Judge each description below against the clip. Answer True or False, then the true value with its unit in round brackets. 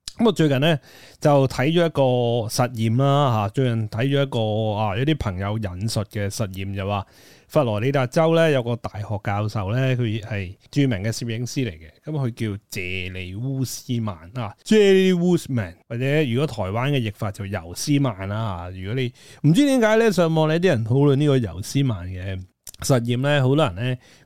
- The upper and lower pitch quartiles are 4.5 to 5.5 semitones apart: True (5.1 semitones)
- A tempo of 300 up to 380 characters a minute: False (290 characters per minute)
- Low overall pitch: True (120 Hz)